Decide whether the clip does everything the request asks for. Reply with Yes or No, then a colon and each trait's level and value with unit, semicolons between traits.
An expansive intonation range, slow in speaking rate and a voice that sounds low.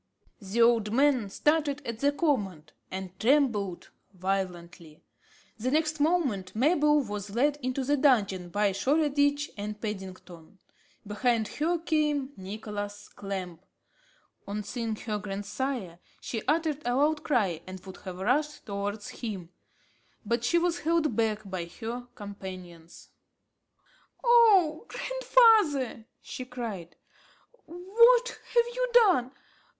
No: wide, 7.0 semitones; slow, 120 wpm; high, 235 Hz